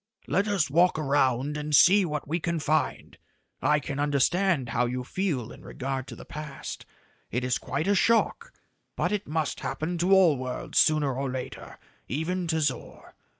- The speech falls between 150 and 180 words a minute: Yes, average, 175 wpm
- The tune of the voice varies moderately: Yes, average, 4.6 semitones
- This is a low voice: No, medium, 150 Hz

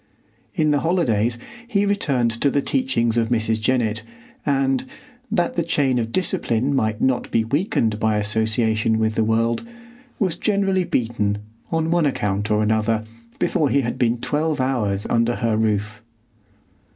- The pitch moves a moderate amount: Yes, average, 4.6 semitones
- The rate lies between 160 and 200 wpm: No, average, 150 wpm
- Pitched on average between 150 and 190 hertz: No, low, 120 Hz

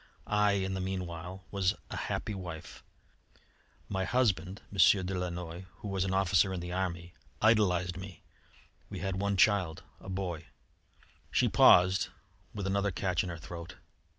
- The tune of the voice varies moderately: No, narrow, 1.8 semitones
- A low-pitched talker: Yes, very low, 95 Hz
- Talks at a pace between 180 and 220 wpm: No, average, 155 wpm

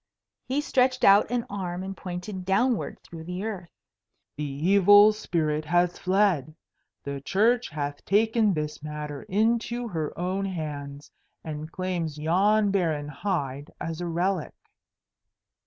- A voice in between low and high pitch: Yes, medium, 180 Hz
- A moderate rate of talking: No, slow, 130 wpm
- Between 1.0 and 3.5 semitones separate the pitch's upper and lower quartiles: No, average, 5.0 semitones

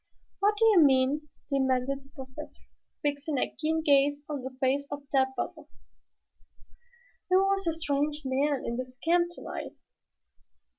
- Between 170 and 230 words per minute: No, average, 145 wpm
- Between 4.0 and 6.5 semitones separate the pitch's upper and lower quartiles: No, average, 3.1 semitones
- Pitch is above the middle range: Yes, very high, 285 Hz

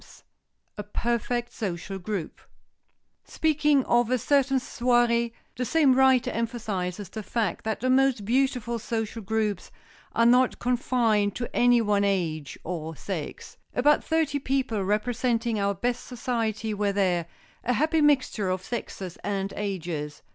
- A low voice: No, high, 230 Hz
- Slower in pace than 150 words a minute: Yes, average, 140 wpm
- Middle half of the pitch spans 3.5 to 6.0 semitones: Yes, average, 3.9 semitones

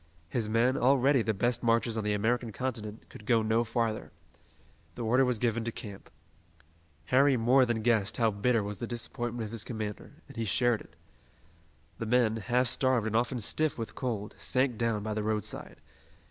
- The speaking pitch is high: No, low, 115 Hz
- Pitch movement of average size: No, narrow, 2.2 semitones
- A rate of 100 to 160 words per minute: No, average, 185 wpm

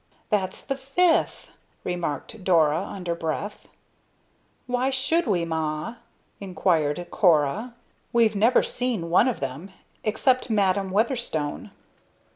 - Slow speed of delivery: Yes, slow, 105 wpm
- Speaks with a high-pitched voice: Yes, high, 195 Hz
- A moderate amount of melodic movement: No, wide, 6.4 semitones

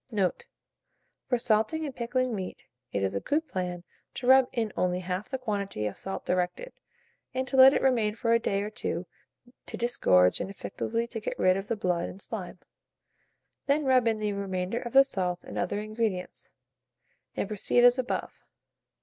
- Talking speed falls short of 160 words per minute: No, average, 185 wpm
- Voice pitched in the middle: No, high, 215 Hz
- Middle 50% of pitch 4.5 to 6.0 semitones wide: Yes, average, 5.0 semitones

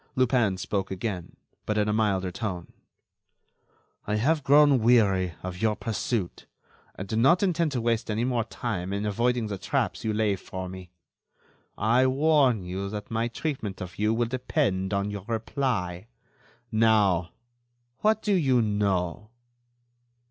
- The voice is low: Yes, low, 110 Hz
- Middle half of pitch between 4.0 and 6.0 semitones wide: Yes, average, 4.3 semitones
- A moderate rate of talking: Yes, average, 150 wpm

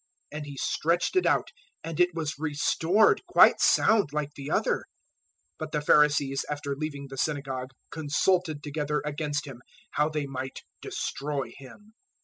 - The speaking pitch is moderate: Yes, medium, 150 Hz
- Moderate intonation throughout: No, narrow, 2.1 semitones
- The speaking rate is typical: Yes, average, 150 wpm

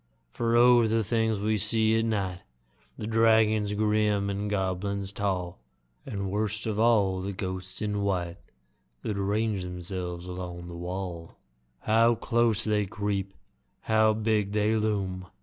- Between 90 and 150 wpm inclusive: Yes, average, 140 wpm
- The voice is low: Yes, low, 105 Hz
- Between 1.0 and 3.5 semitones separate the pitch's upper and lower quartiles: Yes, average, 2.7 semitones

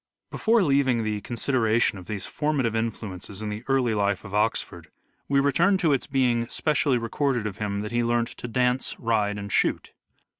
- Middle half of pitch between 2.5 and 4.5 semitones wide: Yes, average, 4.2 semitones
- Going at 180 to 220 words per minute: Yes, average, 190 wpm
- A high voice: No, low, 115 Hz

